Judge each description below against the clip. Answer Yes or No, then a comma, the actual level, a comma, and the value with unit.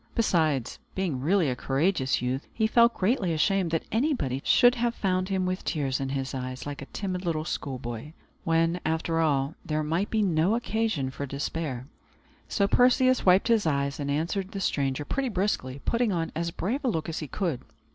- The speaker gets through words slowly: No, average, 185 wpm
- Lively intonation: Yes, wide, 6.1 semitones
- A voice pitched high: No, medium, 165 Hz